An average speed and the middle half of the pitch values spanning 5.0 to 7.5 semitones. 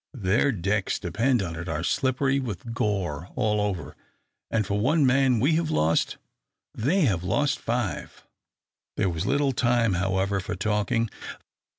Yes: average, 150 wpm; wide, 5.5 semitones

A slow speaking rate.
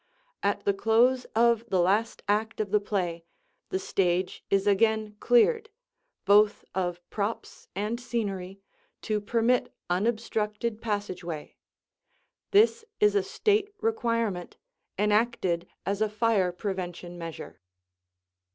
Yes: slow, 115 wpm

